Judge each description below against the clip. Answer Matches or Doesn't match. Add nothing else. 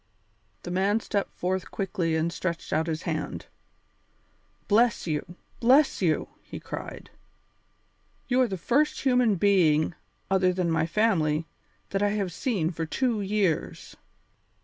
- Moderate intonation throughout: Matches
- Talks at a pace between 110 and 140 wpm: Matches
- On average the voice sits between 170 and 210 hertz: Matches